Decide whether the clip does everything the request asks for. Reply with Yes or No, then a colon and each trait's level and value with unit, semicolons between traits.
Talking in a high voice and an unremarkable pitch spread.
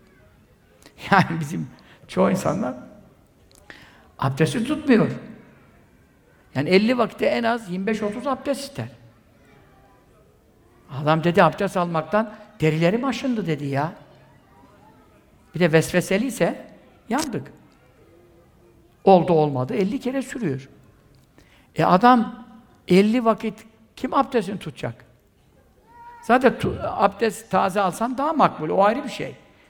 No: high, 200 Hz; wide, 6.9 semitones